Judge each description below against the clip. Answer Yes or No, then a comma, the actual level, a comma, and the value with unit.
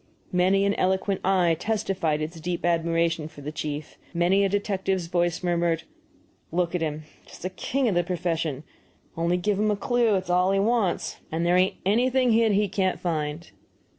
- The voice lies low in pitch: No, medium, 180 Hz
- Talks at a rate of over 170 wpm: Yes, average, 190 wpm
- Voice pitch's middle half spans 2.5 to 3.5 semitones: Yes, average, 2.9 semitones